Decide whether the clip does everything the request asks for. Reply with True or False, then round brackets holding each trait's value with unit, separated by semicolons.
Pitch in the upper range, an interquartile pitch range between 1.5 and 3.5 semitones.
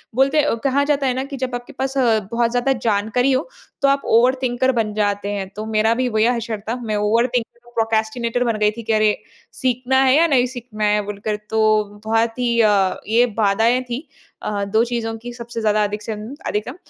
True (230 Hz; 2.8 semitones)